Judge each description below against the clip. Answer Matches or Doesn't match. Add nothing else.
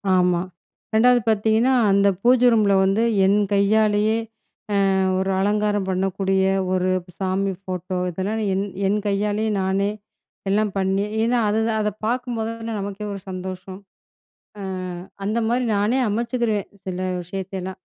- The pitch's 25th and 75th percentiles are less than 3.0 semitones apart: Matches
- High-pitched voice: Matches